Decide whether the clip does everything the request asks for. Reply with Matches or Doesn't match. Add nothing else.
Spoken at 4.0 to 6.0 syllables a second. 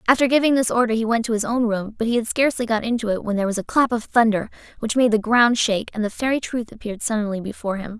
Doesn't match